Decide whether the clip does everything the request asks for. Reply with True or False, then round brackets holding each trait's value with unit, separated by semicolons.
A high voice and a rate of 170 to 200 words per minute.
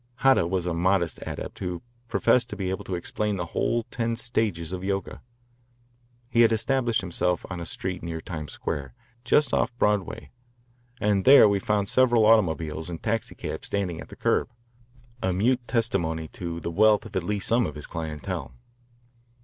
False (95 Hz; 175 wpm)